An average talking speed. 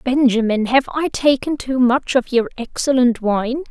Yes: average, 160 wpm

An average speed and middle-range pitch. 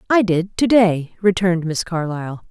Yes: average, 170 wpm; medium, 180 Hz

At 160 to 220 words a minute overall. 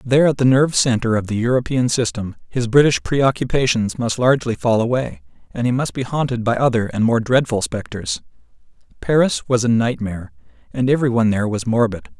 Yes: average, 180 wpm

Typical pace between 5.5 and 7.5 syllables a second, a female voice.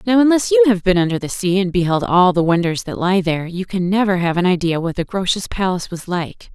Yes: 5.9 syllables/s; female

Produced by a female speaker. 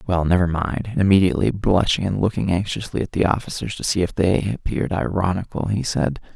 No: male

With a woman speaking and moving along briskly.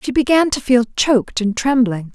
No: female; average, 195 wpm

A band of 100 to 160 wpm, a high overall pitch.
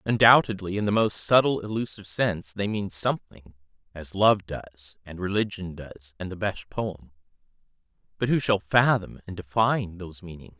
No: average, 145 wpm; very low, 95 Hz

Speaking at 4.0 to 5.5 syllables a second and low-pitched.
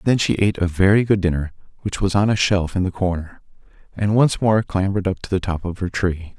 No: 5.9 syllables/s; very low, 95 Hz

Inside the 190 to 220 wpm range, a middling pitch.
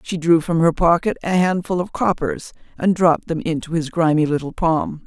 Yes: average, 200 wpm; medium, 165 Hz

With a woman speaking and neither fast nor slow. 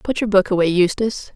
No: female; fast, 220 wpm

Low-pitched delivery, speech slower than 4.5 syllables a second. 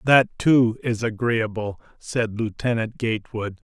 Yes: low, 115 Hz; 4.1 syllables/s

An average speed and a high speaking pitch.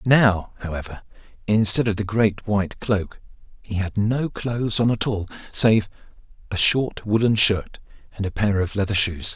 No: average, 165 wpm; low, 105 Hz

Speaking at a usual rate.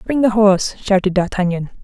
Yes: average, 165 wpm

